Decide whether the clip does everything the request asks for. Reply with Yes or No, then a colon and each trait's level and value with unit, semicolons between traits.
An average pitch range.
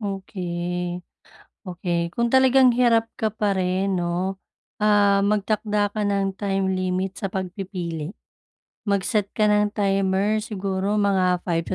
No: narrow, 2.2 semitones